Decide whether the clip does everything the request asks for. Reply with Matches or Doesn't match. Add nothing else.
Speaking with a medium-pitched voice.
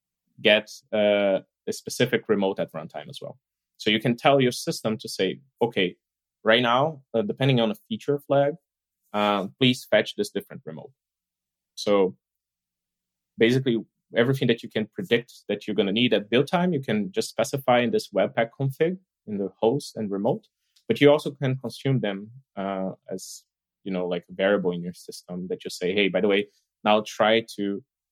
Doesn't match